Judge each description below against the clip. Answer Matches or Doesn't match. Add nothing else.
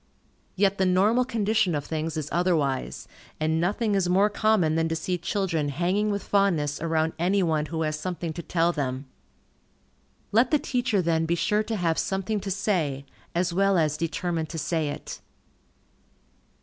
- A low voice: Doesn't match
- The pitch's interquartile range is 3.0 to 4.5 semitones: Matches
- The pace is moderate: Matches